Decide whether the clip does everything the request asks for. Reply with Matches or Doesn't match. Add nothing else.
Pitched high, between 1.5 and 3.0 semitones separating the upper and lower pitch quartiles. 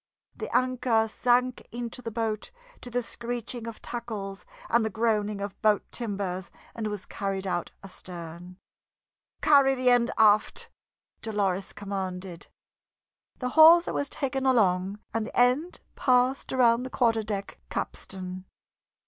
Doesn't match